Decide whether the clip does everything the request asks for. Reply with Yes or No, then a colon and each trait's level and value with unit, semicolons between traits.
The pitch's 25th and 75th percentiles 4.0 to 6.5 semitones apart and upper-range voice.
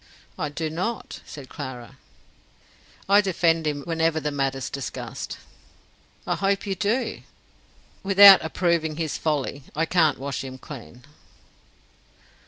No: average, 4.7 semitones; medium, 160 Hz